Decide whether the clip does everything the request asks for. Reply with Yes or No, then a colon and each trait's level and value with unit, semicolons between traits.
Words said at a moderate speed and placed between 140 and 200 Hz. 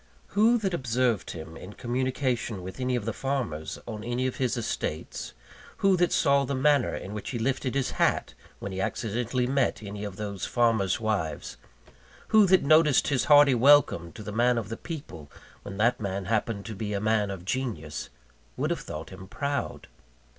No: average, 185 wpm; low, 120 Hz